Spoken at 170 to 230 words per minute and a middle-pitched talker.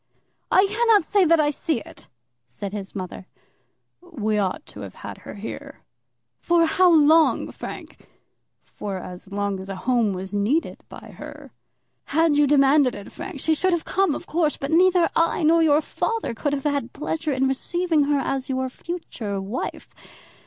No: average, 175 wpm; very high, 290 Hz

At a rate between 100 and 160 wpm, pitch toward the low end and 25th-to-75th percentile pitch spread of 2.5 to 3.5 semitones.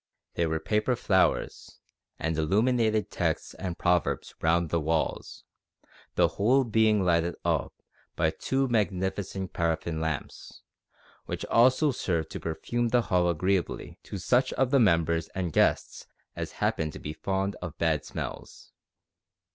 No: average, 140 wpm; very low, 95 Hz; average, 5.2 semitones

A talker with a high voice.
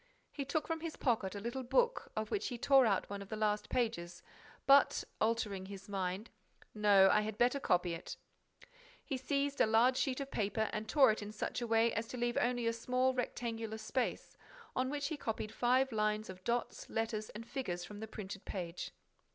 Yes: high, 225 Hz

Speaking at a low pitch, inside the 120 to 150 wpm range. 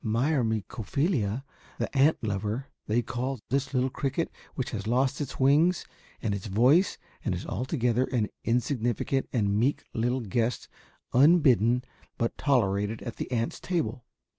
Yes: low, 125 Hz; average, 140 wpm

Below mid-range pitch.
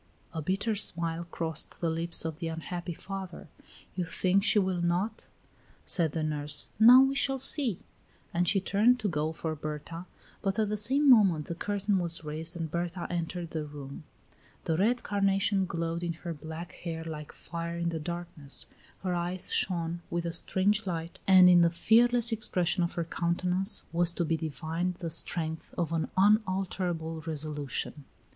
No: medium, 170 Hz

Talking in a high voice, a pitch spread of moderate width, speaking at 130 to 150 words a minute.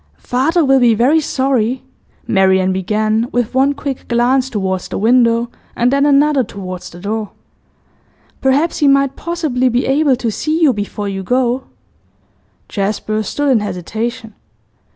Yes: high, 245 Hz; average, 4.2 semitones; average, 145 wpm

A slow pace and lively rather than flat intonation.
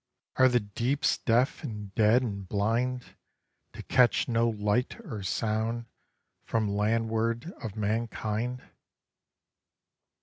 No: slow, 105 wpm; narrow, 2.6 semitones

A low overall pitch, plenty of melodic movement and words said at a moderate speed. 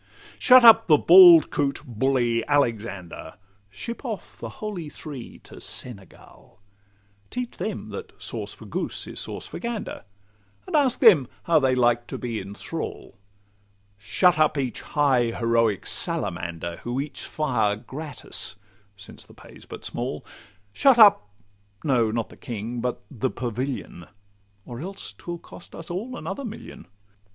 Yes: low, 130 Hz; wide, 7.2 semitones; average, 145 wpm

